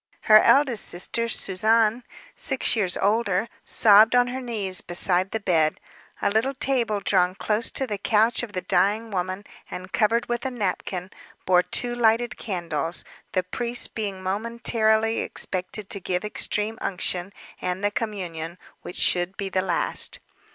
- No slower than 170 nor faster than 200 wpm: No, average, 150 wpm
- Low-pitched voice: No, high, 205 Hz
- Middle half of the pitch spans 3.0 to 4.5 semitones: Yes, average, 3.8 semitones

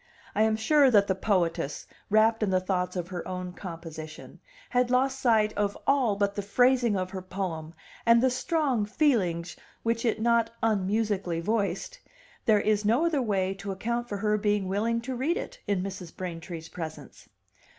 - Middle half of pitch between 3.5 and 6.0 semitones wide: Yes, average, 4.0 semitones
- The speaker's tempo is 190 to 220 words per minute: No, average, 175 wpm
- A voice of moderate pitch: No, high, 205 Hz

